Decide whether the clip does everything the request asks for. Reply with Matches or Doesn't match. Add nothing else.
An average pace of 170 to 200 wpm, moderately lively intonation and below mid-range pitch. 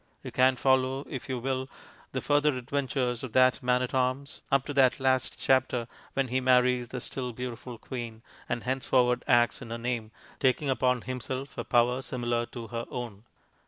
Doesn't match